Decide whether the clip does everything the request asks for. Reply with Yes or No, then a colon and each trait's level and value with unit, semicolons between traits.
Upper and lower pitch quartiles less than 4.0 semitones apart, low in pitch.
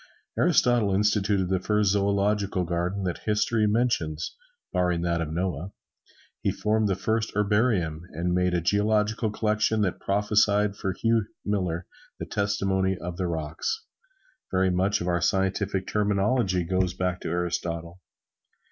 Yes: average, 2.9 semitones; very low, 95 Hz